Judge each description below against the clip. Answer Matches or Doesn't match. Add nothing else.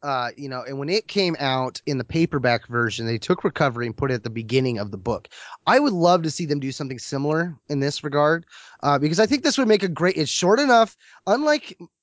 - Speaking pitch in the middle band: Matches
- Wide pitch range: Matches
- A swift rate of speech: Matches